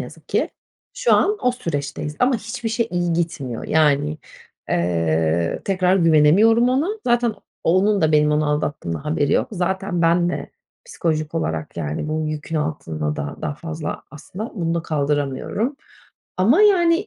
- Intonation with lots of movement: Yes, wide, 6.0 semitones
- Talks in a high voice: No, medium, 165 Hz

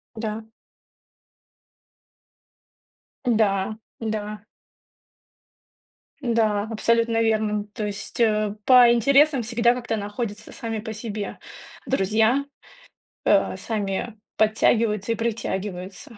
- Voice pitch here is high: Yes, high, 220 Hz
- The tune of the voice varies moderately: No, narrow, 1.9 semitones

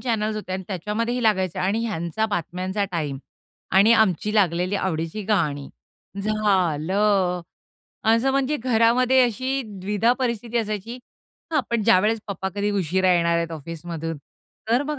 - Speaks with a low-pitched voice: No, high, 205 Hz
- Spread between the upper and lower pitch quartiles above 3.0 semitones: Yes, average, 4.4 semitones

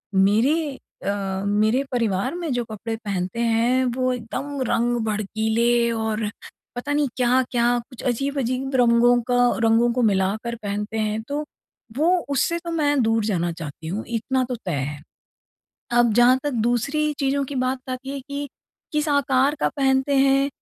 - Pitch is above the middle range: Yes, high, 240 Hz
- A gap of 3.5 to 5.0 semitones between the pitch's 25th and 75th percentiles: Yes, average, 3.8 semitones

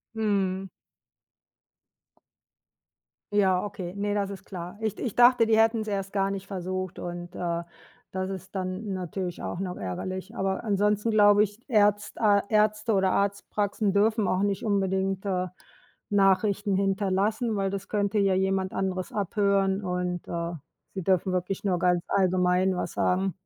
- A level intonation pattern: Yes, narrow, 1.7 semitones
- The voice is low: No, high, 195 Hz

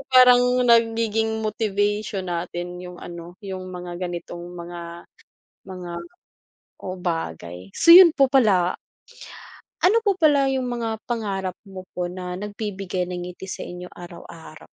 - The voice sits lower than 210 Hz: Yes, medium, 185 Hz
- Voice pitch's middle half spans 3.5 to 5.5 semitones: Yes, average, 4.3 semitones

